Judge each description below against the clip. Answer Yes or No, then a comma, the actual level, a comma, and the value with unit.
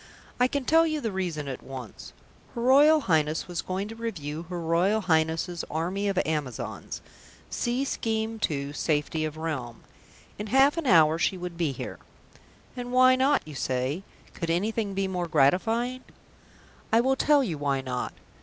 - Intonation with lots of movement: Yes, wide, 7.2 semitones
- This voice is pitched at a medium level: Yes, medium, 180 Hz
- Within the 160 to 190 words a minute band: Yes, average, 165 wpm